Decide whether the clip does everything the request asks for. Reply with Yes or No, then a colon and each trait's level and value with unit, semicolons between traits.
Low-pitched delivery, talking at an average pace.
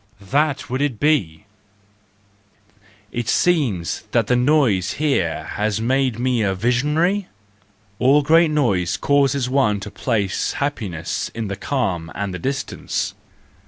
No: low, 125 Hz; slow, 125 wpm